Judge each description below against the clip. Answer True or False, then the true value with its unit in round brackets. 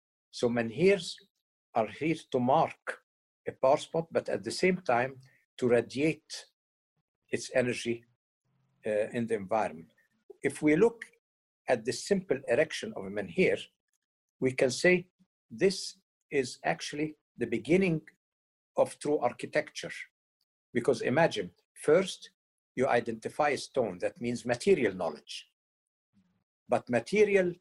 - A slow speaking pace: True (120 wpm)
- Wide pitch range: True (7.2 semitones)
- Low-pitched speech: False (150 Hz)